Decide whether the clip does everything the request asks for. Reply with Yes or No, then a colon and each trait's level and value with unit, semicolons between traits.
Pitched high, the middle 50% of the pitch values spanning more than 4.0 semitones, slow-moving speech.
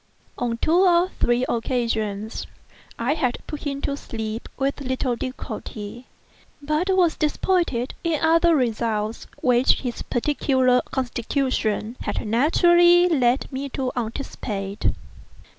Yes: very high, 255 Hz; average, 4.5 semitones; slow, 115 wpm